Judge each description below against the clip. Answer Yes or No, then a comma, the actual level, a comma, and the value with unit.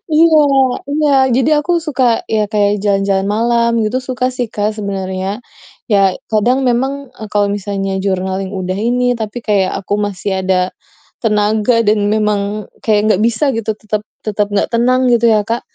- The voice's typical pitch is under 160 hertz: No, high, 215 Hz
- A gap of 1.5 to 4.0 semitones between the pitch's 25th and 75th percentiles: Yes, average, 3.2 semitones